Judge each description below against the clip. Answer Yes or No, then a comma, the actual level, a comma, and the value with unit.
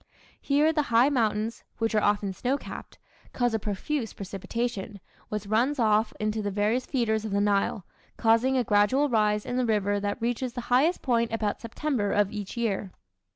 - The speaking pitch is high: Yes, high, 225 Hz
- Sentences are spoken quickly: No, average, 180 wpm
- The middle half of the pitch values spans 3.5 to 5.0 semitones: No, average, 3.0 semitones